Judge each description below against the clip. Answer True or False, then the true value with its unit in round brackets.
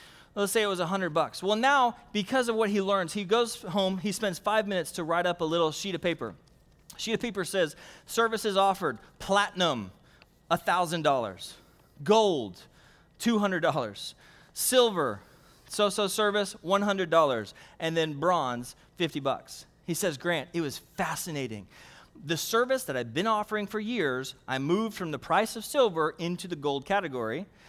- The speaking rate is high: False (155 wpm)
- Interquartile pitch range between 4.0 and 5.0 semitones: True (4.4 semitones)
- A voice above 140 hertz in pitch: True (185 Hz)